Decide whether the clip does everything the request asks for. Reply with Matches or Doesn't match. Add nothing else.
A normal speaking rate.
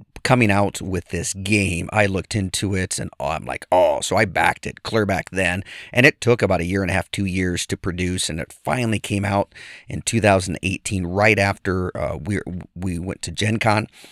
Doesn't match